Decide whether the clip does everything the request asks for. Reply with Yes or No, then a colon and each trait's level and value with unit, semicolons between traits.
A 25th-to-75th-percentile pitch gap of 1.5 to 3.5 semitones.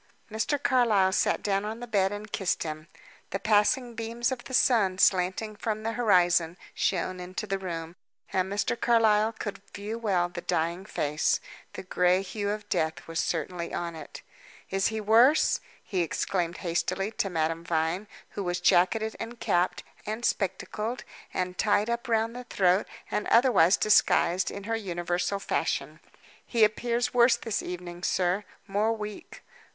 No: average, 3.9 semitones